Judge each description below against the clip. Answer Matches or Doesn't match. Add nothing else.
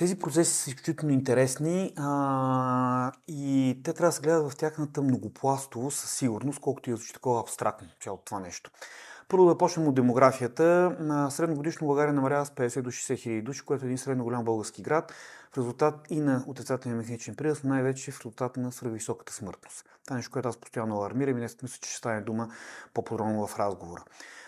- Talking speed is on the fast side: Matches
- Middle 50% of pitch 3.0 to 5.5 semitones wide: Matches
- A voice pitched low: Matches